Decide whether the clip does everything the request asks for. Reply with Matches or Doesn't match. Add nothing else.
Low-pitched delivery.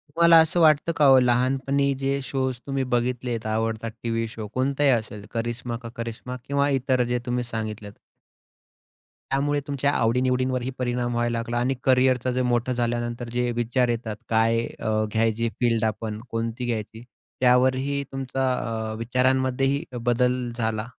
Matches